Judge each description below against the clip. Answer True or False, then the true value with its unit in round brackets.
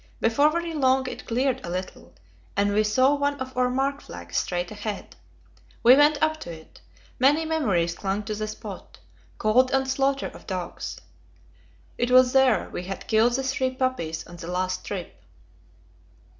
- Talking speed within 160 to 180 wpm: True (170 wpm)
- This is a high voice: True (250 Hz)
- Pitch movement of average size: False (5.7 semitones)